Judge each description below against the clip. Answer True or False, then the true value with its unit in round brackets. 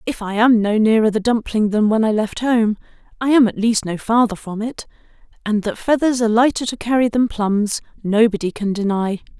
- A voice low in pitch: False (220 Hz)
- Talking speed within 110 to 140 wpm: False (205 wpm)